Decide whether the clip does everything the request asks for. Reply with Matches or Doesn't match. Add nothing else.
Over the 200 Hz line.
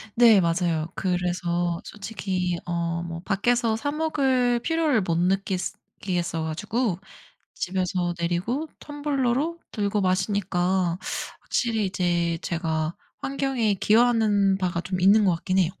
Doesn't match